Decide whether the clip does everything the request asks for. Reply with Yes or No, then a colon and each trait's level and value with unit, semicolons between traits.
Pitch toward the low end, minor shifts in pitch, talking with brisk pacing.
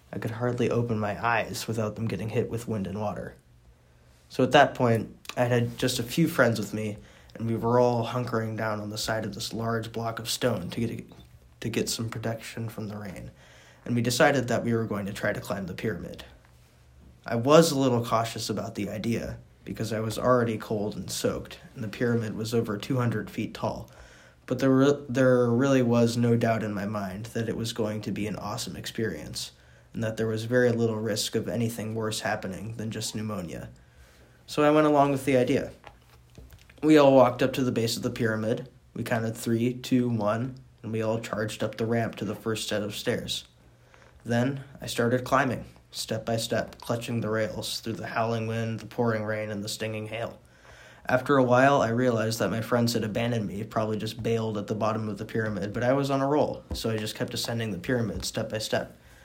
Yes: low, 115 Hz; narrow, 2.2 semitones; fast, 215 wpm